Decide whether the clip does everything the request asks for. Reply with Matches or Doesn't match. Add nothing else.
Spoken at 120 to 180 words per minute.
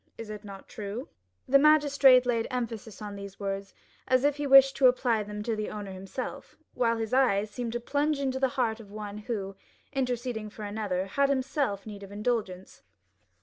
Doesn't match